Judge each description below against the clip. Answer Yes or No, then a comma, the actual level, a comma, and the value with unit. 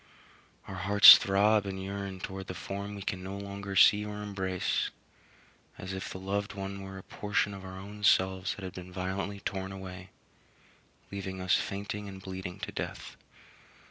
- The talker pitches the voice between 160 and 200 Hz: No, very low, 95 Hz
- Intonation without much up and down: Yes, narrow, 1.1 semitones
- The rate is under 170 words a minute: No, average, 175 wpm